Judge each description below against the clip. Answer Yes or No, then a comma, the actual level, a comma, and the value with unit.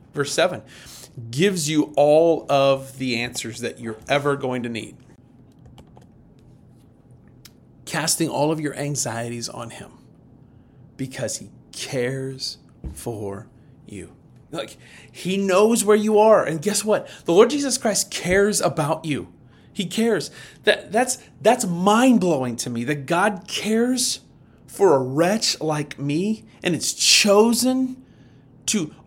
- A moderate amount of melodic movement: No, wide, 7.8 semitones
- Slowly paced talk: Yes, slow, 130 wpm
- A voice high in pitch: No, medium, 150 Hz